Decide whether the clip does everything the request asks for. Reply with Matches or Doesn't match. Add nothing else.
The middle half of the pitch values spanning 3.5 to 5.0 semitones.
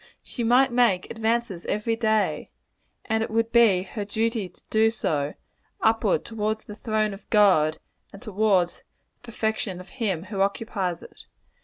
Doesn't match